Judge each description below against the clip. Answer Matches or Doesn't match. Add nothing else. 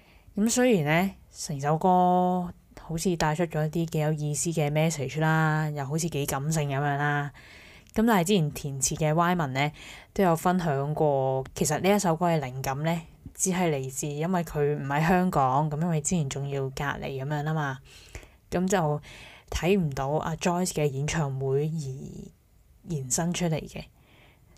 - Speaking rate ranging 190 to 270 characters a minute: Matches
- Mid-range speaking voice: Matches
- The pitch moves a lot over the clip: Doesn't match